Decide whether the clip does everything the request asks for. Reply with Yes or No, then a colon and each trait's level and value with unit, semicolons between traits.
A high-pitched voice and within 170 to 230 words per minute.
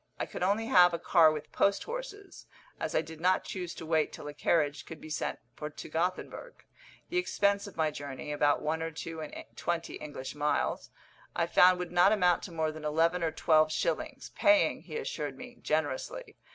No: medium, 165 Hz; average, 200 wpm